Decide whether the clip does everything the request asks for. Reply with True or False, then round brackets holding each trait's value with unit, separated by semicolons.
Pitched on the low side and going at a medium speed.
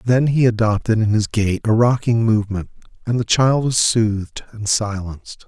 True (110 Hz; 175 wpm)